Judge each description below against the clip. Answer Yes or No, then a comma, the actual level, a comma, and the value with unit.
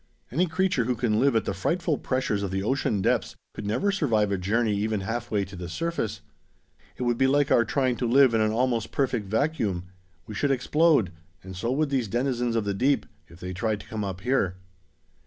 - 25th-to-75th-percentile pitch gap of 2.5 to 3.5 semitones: No, average, 4.9 semitones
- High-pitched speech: No, low, 115 Hz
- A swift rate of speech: Yes, fast, 210 wpm